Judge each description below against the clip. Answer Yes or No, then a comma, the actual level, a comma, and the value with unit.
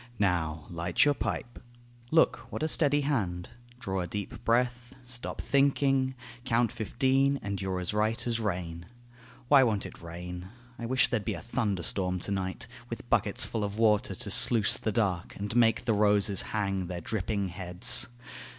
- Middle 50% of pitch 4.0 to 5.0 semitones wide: Yes, average, 4.7 semitones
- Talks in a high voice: No, low, 105 Hz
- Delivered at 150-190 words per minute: Yes, average, 170 wpm